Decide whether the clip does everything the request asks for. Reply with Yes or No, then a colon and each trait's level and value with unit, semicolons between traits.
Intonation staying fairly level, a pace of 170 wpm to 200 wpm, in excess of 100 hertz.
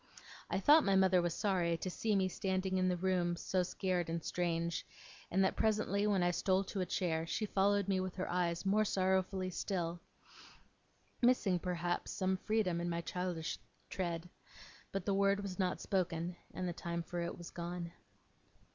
Yes: narrow, 2.0 semitones; average, 180 wpm; medium, 185 Hz